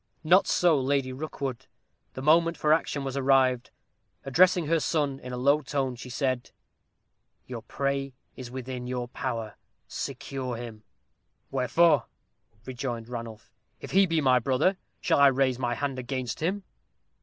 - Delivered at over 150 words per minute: No, average, 145 wpm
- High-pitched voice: No, low, 135 Hz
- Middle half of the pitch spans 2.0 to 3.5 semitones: Yes, average, 2.8 semitones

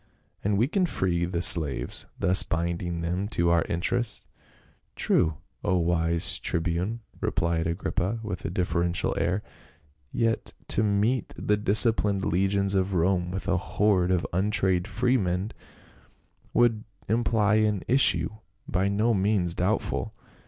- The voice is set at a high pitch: No, very low, 95 Hz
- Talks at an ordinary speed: No, slow, 130 wpm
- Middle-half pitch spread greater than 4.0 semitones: No, average, 3.6 semitones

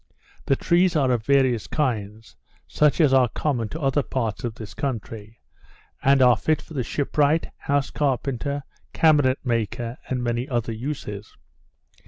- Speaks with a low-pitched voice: Yes, low, 130 Hz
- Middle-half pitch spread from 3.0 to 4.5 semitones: Yes, average, 3.7 semitones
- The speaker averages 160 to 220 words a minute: No, average, 150 wpm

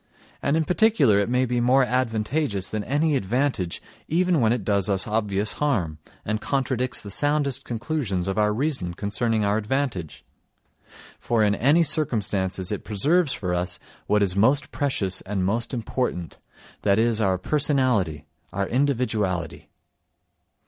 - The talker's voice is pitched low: Yes, low, 110 Hz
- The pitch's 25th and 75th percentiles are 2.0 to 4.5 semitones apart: No, wide, 5.5 semitones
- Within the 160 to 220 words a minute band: No, average, 140 wpm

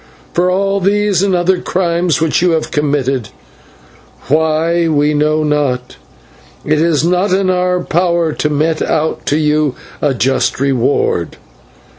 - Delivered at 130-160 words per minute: Yes, average, 140 wpm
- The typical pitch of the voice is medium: Yes, medium, 160 Hz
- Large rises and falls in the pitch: No, average, 3.3 semitones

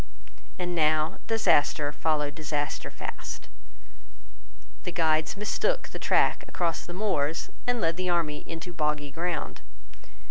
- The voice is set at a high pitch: No, medium, 160 Hz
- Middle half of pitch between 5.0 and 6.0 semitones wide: No, average, 2.8 semitones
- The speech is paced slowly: Yes, slow, 120 wpm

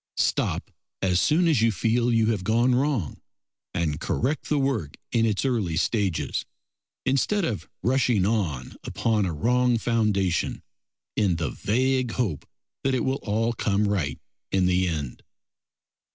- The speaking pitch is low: Yes, low, 110 Hz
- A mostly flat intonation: No, average, 5.2 semitones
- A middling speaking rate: Yes, average, 145 wpm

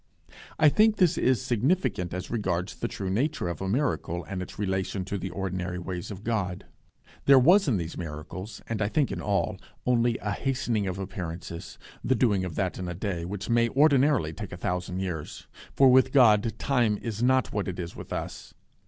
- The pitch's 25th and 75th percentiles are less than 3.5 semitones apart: No, wide, 5.6 semitones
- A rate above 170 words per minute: Yes, average, 195 wpm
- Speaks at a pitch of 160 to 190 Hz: No, low, 100 Hz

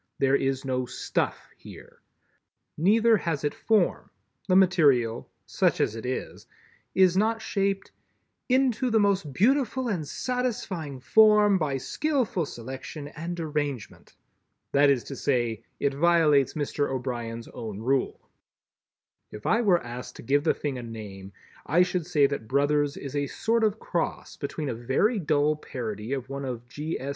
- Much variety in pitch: Yes, wide, 6.7 semitones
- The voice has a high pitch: No, medium, 145 Hz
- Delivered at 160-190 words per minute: No, average, 150 wpm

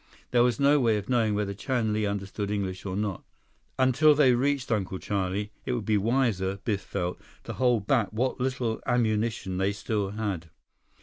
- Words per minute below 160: No, average, 180 wpm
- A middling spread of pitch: Yes, average, 3.7 semitones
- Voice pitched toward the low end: Yes, low, 110 Hz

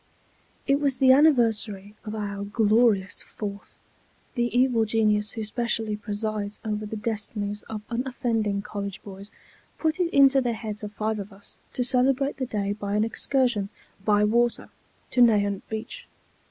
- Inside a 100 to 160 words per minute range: Yes, average, 155 wpm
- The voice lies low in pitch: No, high, 220 Hz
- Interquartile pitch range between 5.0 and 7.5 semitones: No, average, 2.9 semitones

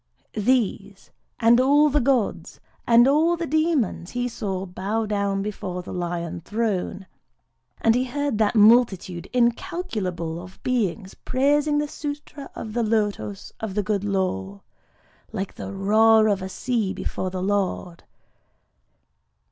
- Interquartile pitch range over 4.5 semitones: Yes, average, 4.9 semitones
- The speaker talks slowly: Yes, slow, 130 wpm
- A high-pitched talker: Yes, high, 215 Hz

